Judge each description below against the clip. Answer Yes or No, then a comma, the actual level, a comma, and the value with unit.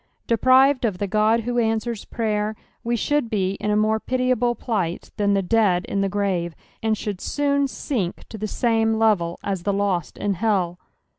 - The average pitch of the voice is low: No, high, 215 Hz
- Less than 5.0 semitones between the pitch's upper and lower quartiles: Yes, average, 2.9 semitones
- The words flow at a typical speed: Yes, average, 180 wpm